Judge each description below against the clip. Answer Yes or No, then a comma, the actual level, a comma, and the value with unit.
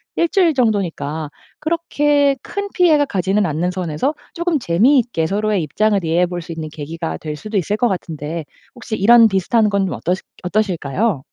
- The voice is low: No, high, 200 Hz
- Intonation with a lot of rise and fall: Yes, wide, 6.6 semitones